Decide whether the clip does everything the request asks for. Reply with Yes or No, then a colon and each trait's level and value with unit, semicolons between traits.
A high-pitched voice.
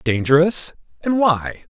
No: medium, 160 Hz